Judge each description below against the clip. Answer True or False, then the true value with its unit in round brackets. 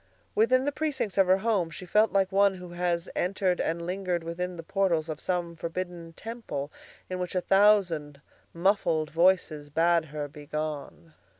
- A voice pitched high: False (180 Hz)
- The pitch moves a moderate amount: True (3.0 semitones)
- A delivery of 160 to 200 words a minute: True (165 wpm)